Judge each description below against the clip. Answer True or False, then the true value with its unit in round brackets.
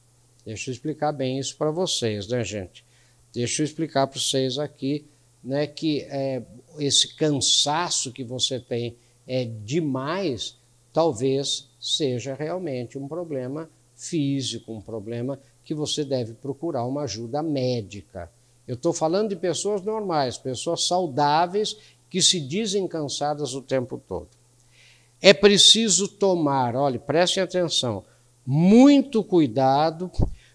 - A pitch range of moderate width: True (5.0 semitones)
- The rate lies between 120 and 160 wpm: True (125 wpm)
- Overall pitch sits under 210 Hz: True (140 Hz)